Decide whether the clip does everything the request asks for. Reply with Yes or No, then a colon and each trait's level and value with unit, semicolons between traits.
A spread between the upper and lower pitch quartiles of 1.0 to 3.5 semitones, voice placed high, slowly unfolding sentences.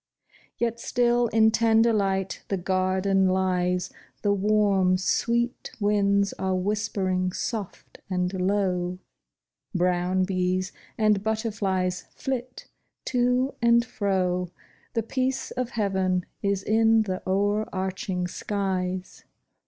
Yes: average, 3.1 semitones; high, 195 Hz; slow, 105 wpm